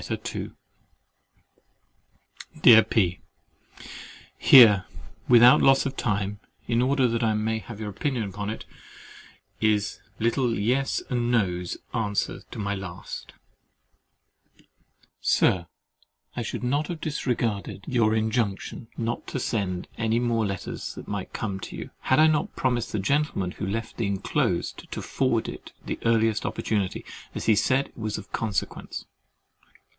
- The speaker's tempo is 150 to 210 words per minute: No, average, 140 wpm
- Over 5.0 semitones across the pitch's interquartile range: No, average, 3.2 semitones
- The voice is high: No, low, 110 Hz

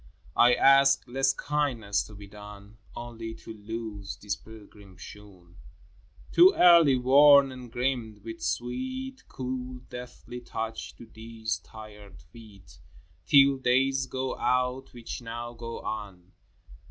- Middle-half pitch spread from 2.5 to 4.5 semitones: Yes, average, 4.0 semitones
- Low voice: Yes, low, 120 Hz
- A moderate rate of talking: No, slow, 130 wpm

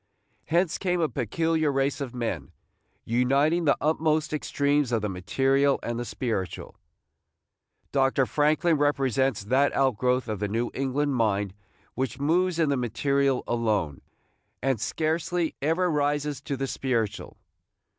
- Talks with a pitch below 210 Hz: Yes, low, 135 Hz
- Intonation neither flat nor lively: Yes, average, 4.0 semitones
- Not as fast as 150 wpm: Yes, slow, 135 wpm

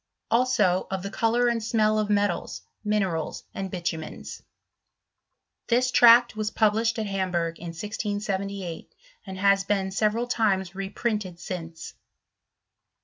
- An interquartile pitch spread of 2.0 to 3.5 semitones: Yes, average, 2.7 semitones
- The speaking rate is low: Yes, slow, 125 wpm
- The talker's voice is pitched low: No, high, 200 Hz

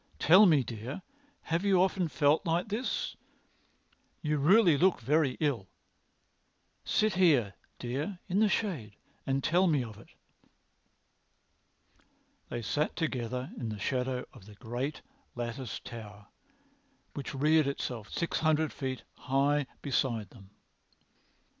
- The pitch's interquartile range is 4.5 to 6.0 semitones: Yes, average, 5.3 semitones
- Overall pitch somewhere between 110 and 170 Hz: Yes, medium, 140 Hz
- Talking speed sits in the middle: No, slow, 125 wpm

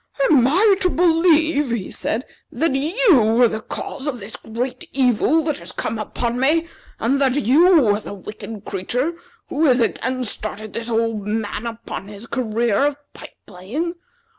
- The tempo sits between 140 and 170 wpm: Yes, average, 165 wpm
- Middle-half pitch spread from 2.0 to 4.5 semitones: No, average, 5.3 semitones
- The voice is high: Yes, very high, 250 Hz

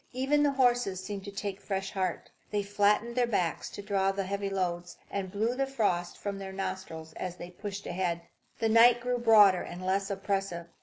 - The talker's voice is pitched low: No, high, 195 Hz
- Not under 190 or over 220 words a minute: Yes, average, 195 wpm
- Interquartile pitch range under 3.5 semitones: Yes, average, 2.8 semitones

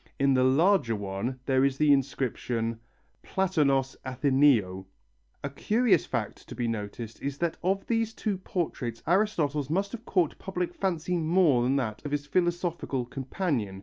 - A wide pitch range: Yes, wide, 6.2 semitones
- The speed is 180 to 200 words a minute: No, average, 150 wpm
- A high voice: No, medium, 140 Hz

